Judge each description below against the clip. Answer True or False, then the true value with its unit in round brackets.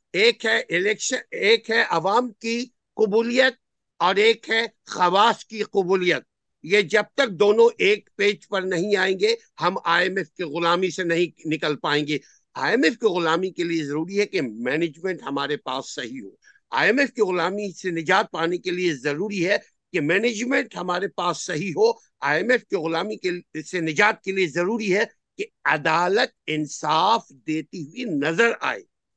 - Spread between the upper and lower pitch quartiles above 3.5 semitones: True (5.6 semitones)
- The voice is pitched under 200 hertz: True (190 Hz)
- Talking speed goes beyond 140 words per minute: True (175 wpm)